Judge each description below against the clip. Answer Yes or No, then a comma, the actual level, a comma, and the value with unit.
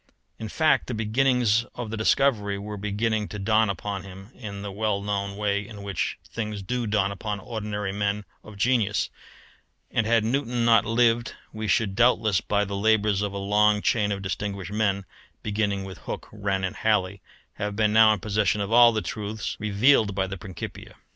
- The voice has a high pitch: No, low, 105 Hz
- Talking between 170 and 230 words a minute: Yes, average, 185 wpm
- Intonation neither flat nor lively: No, narrow, 1.8 semitones